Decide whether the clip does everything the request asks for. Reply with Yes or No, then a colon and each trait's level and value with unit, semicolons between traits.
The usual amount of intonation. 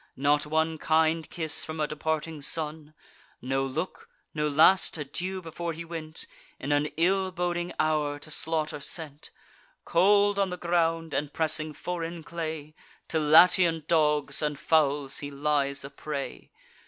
No: narrow, 2.1 semitones